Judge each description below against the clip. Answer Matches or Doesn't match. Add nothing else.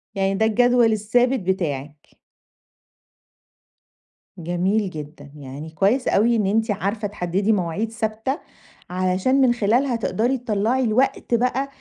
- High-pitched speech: Matches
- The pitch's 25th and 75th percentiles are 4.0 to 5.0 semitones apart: Matches